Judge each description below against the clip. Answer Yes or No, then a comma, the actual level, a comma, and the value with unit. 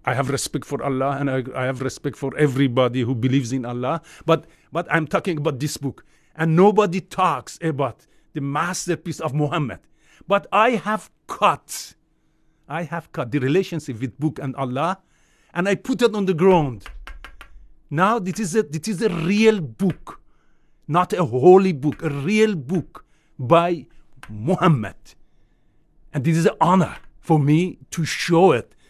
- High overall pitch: No, medium, 160 Hz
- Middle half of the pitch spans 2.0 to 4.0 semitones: No, average, 4.9 semitones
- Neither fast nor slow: Yes, average, 165 wpm